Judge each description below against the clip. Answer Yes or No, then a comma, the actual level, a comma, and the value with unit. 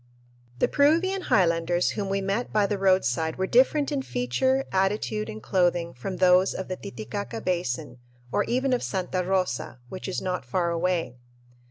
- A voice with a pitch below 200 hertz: Yes, medium, 185 Hz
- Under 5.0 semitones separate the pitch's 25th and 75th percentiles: Yes, average, 3.7 semitones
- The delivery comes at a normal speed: Yes, average, 165 wpm